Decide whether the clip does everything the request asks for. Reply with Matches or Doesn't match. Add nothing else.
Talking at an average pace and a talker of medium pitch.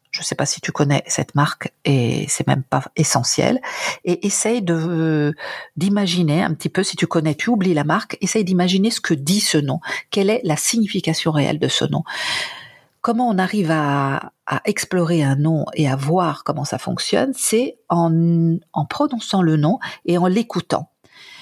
Matches